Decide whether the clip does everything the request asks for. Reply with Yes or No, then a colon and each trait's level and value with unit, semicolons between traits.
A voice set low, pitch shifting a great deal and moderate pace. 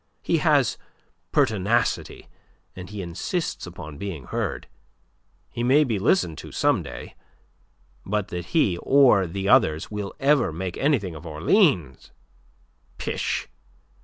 No: low, 100 Hz; wide, 6.4 semitones; slow, 125 wpm